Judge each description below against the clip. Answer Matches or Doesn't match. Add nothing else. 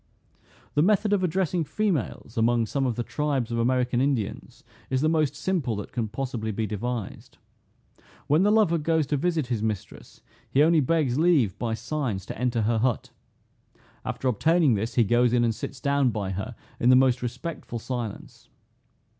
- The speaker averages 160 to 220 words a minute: Matches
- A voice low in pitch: Matches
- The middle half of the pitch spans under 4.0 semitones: Doesn't match